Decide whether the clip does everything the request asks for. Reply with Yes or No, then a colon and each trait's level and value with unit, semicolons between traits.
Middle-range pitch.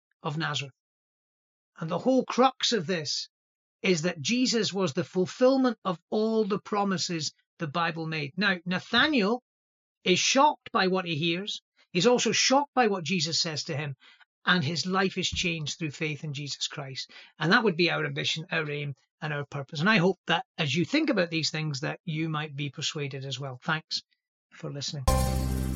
Yes: medium, 170 Hz